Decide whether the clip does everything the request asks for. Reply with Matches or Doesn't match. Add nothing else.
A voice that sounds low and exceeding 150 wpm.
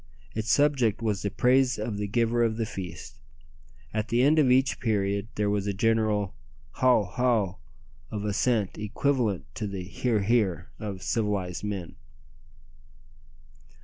Doesn't match